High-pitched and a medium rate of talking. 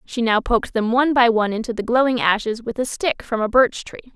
No: high, 235 Hz; fast, 260 wpm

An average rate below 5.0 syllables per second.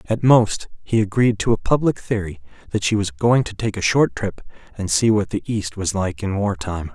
No: 5.1 syllables/s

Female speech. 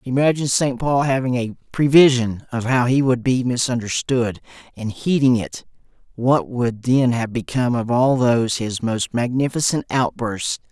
No: male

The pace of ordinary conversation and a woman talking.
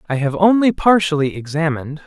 No: average, 145 wpm; male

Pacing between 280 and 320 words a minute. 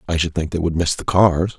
Yes: fast, 305 wpm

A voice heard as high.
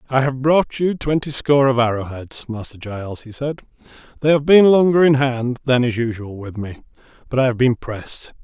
No: low, 130 Hz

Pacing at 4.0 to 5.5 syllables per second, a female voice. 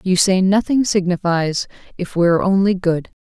Yes: 5.1 syllables/s; female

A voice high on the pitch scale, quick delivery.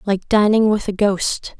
No: high, 205 Hz; average, 190 wpm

